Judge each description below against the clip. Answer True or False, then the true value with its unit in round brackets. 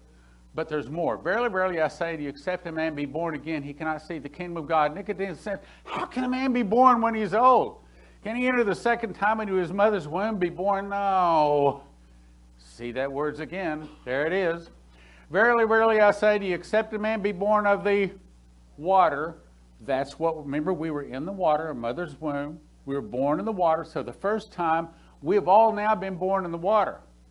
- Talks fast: True (215 wpm)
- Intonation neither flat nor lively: False (6.2 semitones)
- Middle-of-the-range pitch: True (170 Hz)